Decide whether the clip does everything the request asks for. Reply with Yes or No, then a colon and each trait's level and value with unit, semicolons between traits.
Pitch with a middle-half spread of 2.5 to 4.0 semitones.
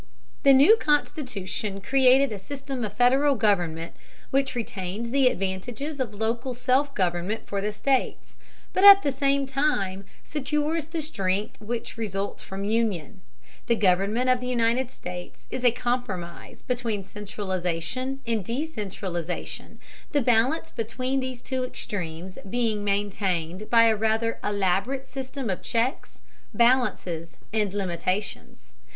No: average, 5.1 semitones